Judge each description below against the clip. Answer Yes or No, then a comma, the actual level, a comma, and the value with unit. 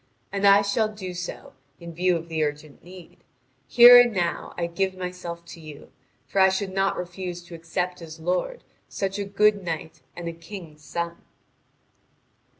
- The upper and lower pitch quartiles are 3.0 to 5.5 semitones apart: No, narrow, 2.5 semitones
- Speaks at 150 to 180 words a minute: Yes, average, 170 wpm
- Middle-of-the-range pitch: Yes, medium, 180 Hz